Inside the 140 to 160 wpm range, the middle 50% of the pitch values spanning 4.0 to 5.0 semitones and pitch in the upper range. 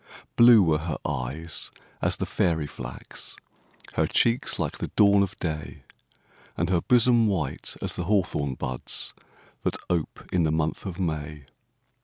No: average, 150 wpm; average, 4.6 semitones; very low, 85 Hz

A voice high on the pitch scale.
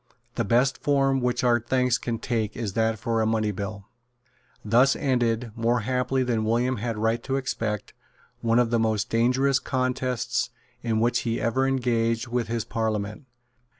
No: low, 120 Hz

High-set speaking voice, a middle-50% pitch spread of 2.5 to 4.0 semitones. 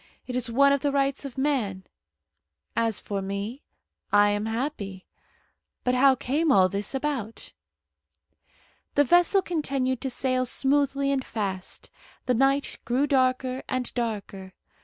No: very high, 255 Hz; average, 4.4 semitones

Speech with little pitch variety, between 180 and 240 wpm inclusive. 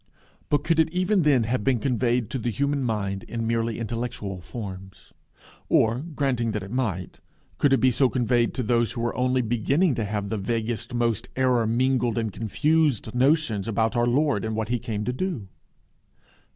No: average, 3.1 semitones; average, 185 wpm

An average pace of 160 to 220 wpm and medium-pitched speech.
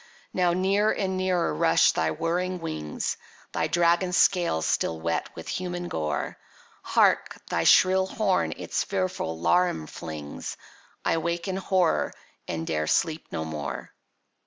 No: slow, 135 wpm; medium, 170 Hz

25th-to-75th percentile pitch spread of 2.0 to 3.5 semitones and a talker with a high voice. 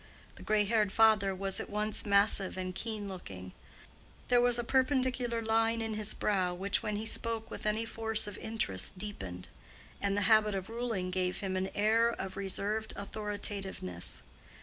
Yes: average, 2.7 semitones; high, 210 Hz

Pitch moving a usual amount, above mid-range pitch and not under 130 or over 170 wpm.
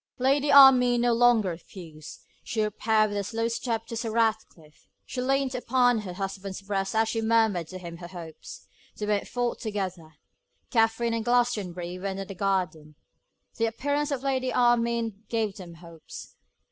Yes: average, 4.3 semitones; high, 220 Hz; average, 165 wpm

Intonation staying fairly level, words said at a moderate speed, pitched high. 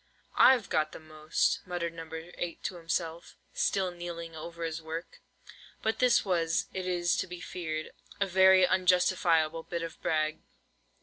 No: narrow, 2.1 semitones; average, 150 wpm; medium, 170 Hz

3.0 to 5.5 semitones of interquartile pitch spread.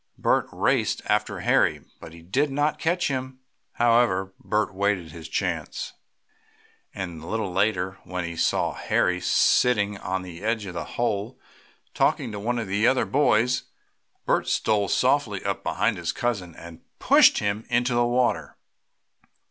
Yes: average, 4.7 semitones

